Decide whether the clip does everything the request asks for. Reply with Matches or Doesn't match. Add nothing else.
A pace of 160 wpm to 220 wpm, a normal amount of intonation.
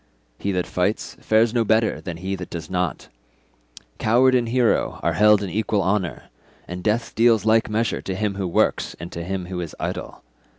Matches